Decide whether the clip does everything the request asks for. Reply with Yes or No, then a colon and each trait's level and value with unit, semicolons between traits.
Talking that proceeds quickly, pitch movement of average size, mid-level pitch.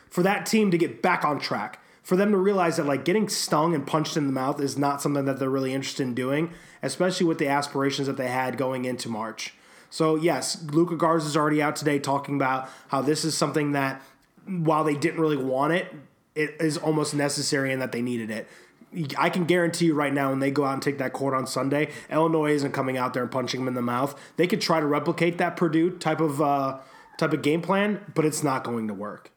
Yes: fast, 240 wpm; average, 3.5 semitones; medium, 145 Hz